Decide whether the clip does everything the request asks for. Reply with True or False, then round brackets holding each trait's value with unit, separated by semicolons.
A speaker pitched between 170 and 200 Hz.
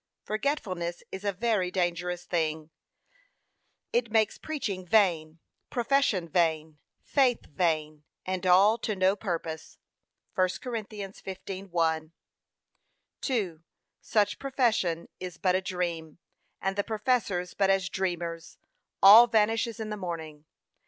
True (185 Hz)